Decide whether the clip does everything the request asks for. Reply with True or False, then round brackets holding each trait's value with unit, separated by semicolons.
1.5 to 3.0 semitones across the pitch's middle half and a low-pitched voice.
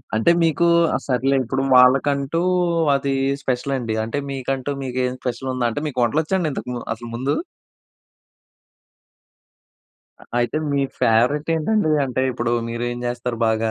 True (2.6 semitones; 130 Hz)